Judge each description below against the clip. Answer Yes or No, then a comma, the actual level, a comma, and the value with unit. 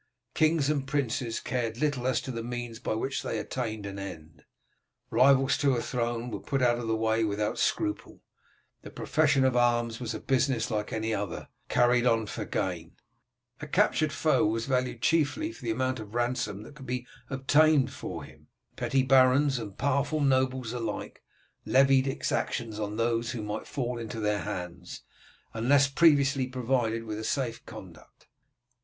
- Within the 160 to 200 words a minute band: Yes, average, 170 wpm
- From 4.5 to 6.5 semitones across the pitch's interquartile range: No, average, 3.1 semitones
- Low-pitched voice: Yes, low, 120 Hz